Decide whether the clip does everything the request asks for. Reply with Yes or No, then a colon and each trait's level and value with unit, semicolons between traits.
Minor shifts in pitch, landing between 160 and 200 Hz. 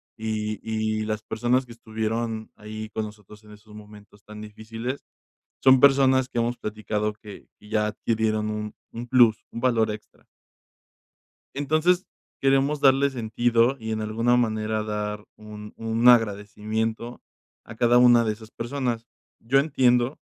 No: narrow, 2.3 semitones; low, 110 Hz